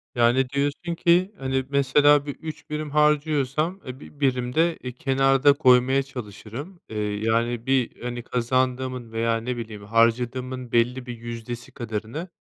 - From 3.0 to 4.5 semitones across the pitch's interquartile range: Yes, average, 3.4 semitones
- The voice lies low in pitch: Yes, low, 130 Hz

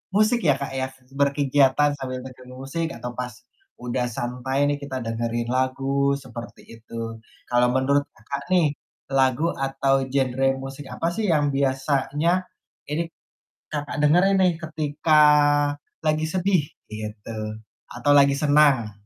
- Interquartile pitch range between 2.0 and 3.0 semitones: Yes, average, 2.7 semitones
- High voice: No, medium, 140 Hz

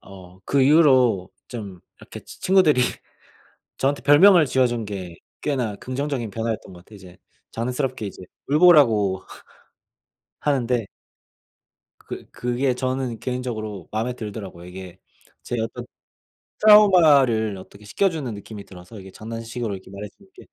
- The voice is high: No, low, 115 Hz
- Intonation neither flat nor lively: Yes, average, 5.0 semitones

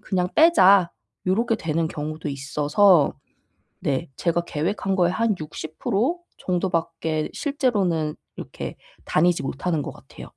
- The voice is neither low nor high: Yes, medium, 170 Hz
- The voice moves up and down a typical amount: Yes, average, 4.2 semitones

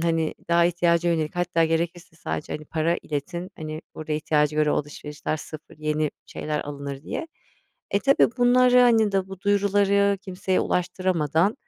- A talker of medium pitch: Yes, medium, 170 Hz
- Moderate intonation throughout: Yes, average, 4.0 semitones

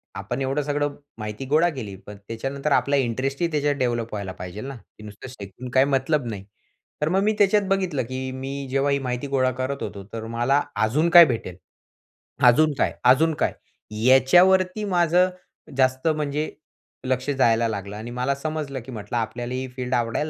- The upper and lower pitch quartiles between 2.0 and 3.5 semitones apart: No, average, 3.9 semitones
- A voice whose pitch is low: Yes, low, 130 Hz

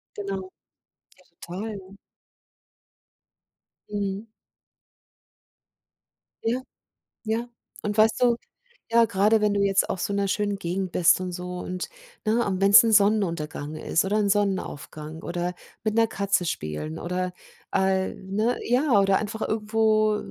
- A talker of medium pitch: No, high, 200 Hz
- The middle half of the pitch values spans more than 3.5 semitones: No, average, 2.8 semitones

